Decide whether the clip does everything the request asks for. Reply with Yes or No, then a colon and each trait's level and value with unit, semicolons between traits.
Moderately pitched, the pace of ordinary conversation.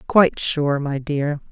Yes: medium, 150 Hz; average, 160 wpm